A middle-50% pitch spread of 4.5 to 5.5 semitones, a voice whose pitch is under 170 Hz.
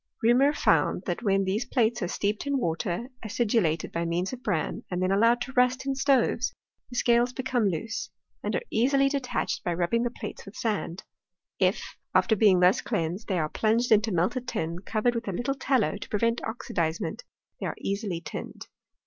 No: average, 5.0 semitones; high, 220 Hz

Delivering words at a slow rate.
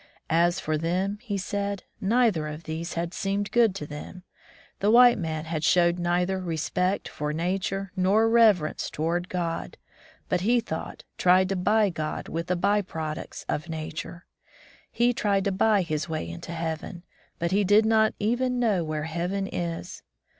No: average, 165 wpm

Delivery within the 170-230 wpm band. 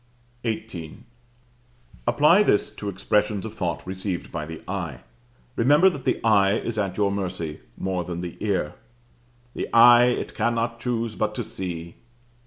No: average, 145 wpm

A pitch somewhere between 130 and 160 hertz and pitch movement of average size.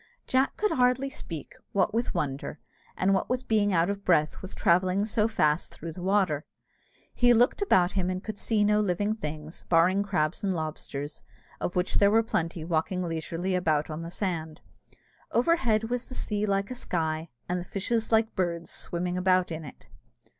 No: medium, 185 Hz; average, 4.4 semitones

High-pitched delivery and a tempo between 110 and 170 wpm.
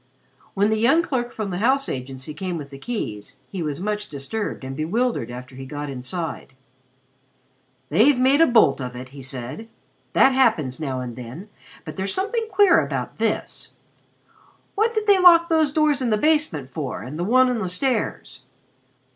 No: high, 200 Hz; average, 180 wpm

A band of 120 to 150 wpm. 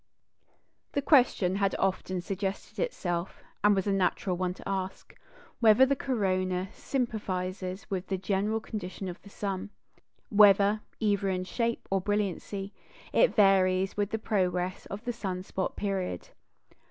Yes: average, 140 wpm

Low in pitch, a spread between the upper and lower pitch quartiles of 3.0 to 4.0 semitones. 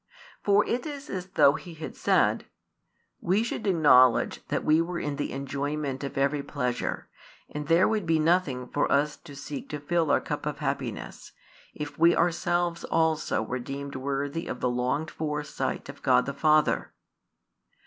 No: medium, 150 Hz; average, 3.5 semitones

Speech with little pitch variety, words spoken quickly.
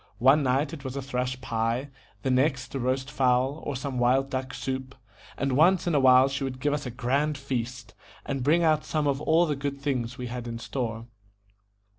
Yes: narrow, 2.1 semitones; fast, 210 wpm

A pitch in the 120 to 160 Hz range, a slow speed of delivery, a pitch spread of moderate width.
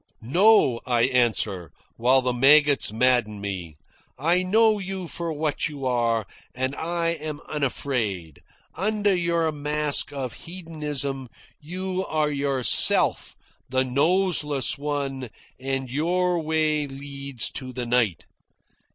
Yes: medium, 140 Hz; slow, 115 wpm; average, 4.5 semitones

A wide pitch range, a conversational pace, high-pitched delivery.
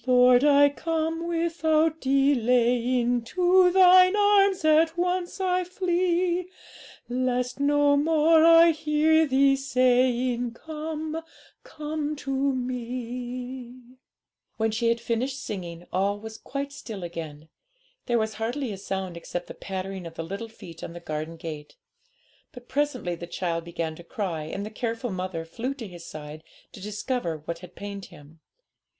Yes: wide, 7.9 semitones; average, 145 wpm; very high, 250 Hz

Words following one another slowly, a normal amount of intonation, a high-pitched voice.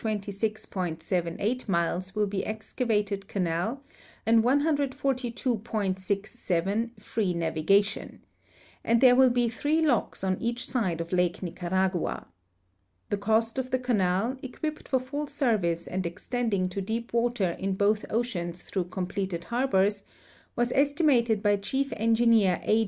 Yes: slow, 130 wpm; average, 4.4 semitones; high, 215 Hz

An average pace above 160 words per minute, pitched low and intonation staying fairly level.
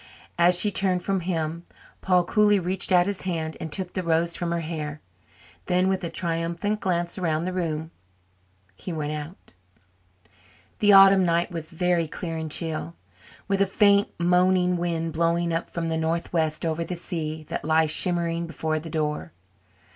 No: average, 170 wpm; medium, 170 Hz; narrow, 2.1 semitones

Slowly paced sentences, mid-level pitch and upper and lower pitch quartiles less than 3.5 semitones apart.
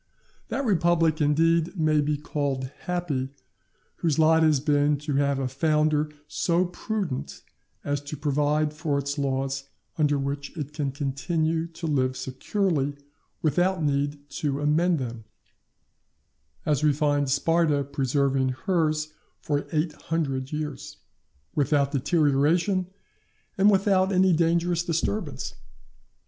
Yes: slow, 120 wpm; medium, 150 Hz; average, 2.8 semitones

